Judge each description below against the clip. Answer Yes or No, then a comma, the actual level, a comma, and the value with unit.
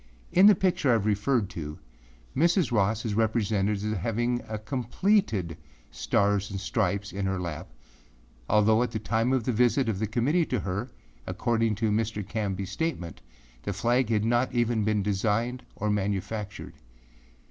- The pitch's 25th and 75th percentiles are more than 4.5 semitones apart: No, average, 3.1 semitones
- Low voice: Yes, low, 110 Hz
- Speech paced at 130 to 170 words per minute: Yes, average, 160 wpm